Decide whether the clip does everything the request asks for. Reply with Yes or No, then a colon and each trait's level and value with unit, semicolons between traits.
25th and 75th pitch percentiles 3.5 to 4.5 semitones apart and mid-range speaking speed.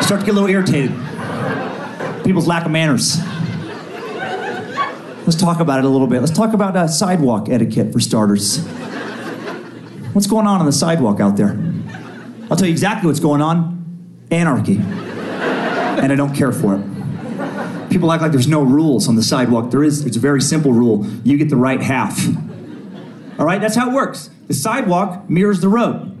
No: average, 5.3 semitones; average, 180 wpm